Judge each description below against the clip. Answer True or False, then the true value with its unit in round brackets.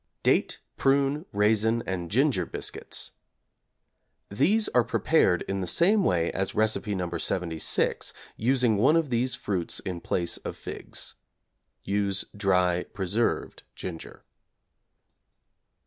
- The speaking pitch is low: True (105 Hz)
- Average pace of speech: False (115 wpm)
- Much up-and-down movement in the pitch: True (5.8 semitones)